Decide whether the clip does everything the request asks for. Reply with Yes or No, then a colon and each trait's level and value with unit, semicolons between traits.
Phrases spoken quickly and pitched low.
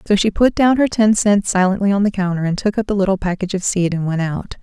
No: fast, 285 wpm; high, 195 Hz